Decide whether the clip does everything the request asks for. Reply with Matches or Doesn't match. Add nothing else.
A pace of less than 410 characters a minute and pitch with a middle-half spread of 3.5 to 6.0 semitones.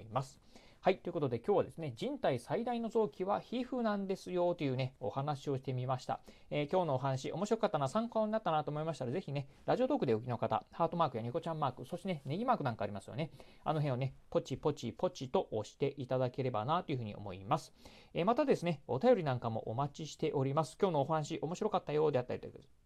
Doesn't match